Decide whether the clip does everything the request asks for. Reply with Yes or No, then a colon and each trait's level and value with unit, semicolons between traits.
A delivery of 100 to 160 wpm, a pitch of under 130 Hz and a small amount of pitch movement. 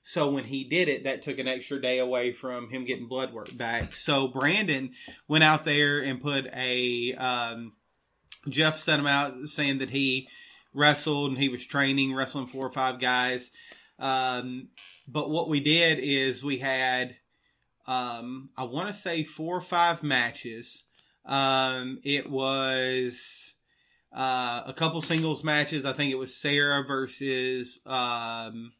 No: average, 155 wpm; low, 135 Hz; narrow, 2.3 semitones